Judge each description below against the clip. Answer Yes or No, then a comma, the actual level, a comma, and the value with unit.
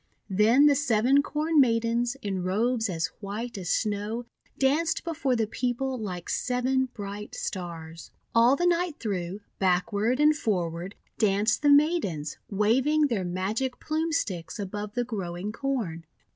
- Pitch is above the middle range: Yes, high, 225 Hz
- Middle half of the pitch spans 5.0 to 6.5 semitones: Yes, wide, 5.5 semitones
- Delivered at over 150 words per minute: No, average, 140 wpm